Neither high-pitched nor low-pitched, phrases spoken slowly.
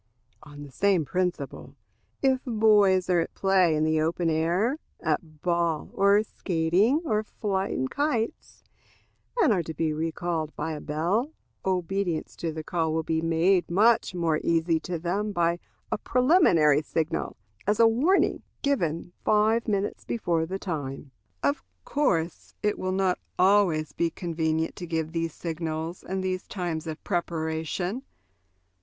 No: medium, 175 Hz; average, 145 wpm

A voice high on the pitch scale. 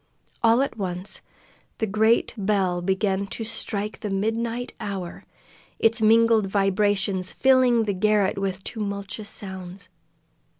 Yes: high, 205 Hz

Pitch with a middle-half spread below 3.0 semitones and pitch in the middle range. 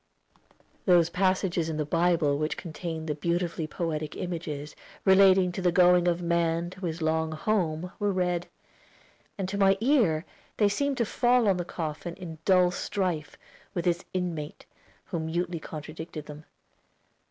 Yes: narrow, 2.6 semitones; medium, 175 Hz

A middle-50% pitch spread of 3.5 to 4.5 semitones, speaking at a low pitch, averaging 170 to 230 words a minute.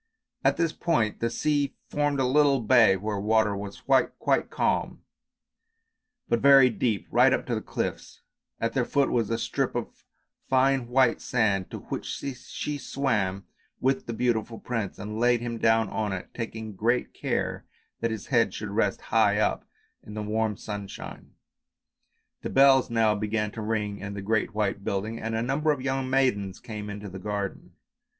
Yes: average, 3.8 semitones; low, 115 Hz; average, 175 wpm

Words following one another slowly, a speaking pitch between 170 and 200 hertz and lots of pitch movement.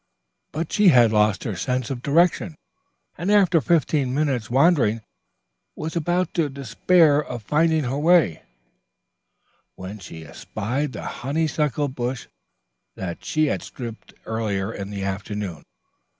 No: slow, 130 wpm; low, 135 Hz; wide, 6.6 semitones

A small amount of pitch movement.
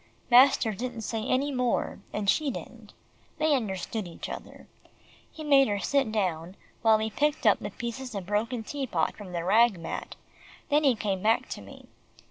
No: average, 4.6 semitones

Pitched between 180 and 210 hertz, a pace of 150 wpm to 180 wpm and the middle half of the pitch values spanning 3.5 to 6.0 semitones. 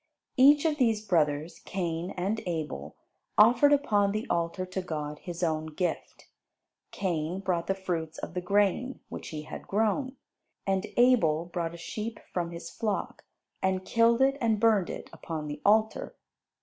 Yes: high, 190 Hz; average, 160 wpm; average, 4.8 semitones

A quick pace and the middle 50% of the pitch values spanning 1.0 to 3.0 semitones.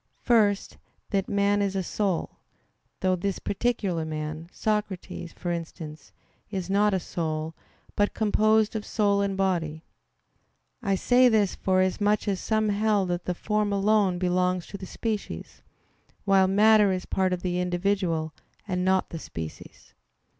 No: average, 145 wpm; narrow, 2.6 semitones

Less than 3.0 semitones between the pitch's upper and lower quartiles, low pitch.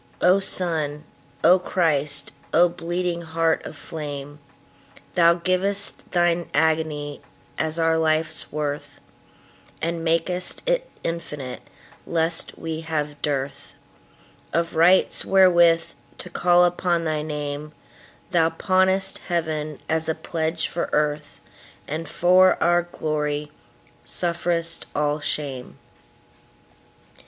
No: narrow, 2.6 semitones; medium, 160 Hz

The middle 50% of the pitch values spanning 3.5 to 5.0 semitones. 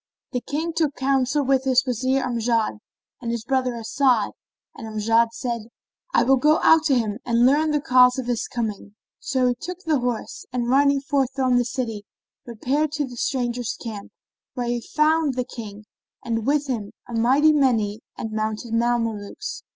No: average, 3.0 semitones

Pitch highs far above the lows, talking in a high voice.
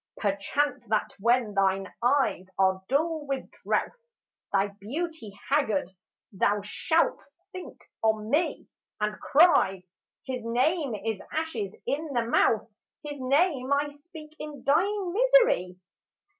Yes: wide, 6.7 semitones; very high, 265 Hz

